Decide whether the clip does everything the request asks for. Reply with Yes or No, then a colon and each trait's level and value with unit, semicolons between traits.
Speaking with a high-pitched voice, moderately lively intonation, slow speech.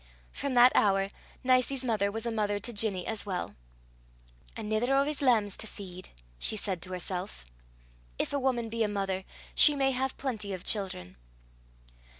No: high, 215 Hz; average, 4.5 semitones; average, 165 wpm